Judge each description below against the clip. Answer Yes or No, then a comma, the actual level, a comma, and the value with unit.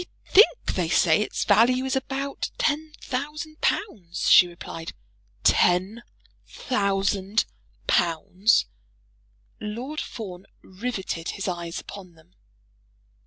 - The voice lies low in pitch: No, high, 205 Hz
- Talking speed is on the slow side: Yes, slow, 105 wpm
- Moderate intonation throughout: No, wide, 6.7 semitones